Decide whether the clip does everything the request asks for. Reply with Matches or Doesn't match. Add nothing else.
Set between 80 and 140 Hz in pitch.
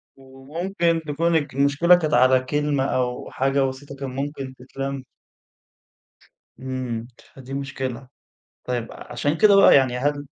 Matches